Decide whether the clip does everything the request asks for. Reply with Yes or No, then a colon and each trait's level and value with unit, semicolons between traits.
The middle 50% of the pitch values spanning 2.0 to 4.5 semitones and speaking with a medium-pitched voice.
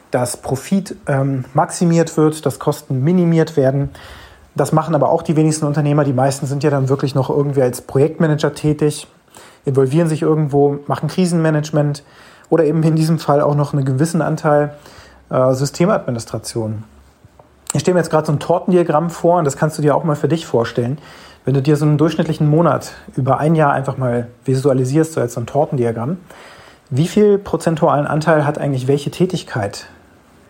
Yes: average, 2.8 semitones; medium, 150 Hz